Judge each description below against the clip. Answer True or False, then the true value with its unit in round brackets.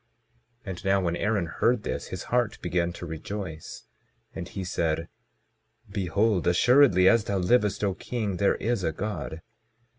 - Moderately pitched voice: False (95 Hz)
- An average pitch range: True (3.3 semitones)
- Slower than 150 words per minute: False (155 wpm)